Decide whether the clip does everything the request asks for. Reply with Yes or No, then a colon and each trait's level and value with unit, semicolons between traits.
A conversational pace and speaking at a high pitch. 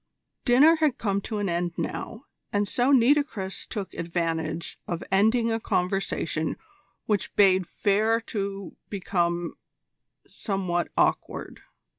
No: slow, 115 wpm; high, 200 Hz